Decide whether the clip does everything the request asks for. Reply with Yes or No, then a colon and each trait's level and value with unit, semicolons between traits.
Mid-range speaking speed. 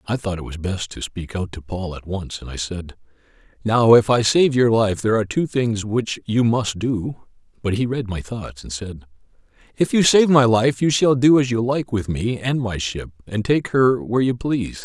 No: fast, 235 wpm